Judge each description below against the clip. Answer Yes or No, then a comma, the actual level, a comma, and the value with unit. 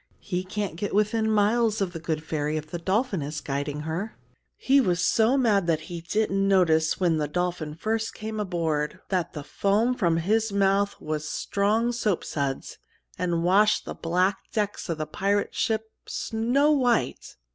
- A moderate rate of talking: Yes, average, 170 wpm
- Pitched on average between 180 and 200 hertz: Yes, high, 190 Hz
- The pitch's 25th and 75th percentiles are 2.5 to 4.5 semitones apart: No, average, 4.9 semitones